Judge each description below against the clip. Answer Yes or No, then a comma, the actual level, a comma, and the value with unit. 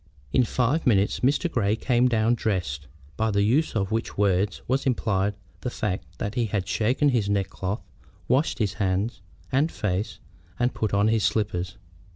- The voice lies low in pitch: Yes, low, 110 Hz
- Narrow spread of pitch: No, average, 3.6 semitones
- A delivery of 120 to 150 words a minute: No, average, 170 wpm